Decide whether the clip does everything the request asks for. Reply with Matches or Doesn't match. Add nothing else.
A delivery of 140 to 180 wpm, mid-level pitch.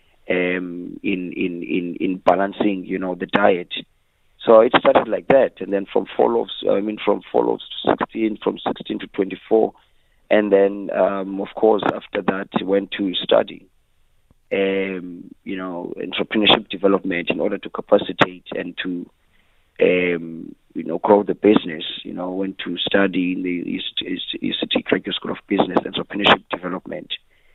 Doesn't match